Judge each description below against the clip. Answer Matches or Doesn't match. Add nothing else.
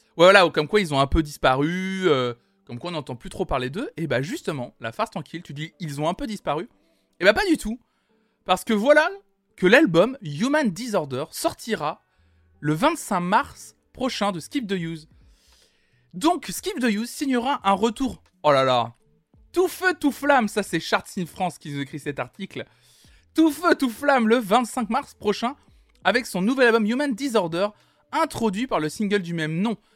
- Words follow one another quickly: Doesn't match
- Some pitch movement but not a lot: Doesn't match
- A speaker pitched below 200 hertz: Doesn't match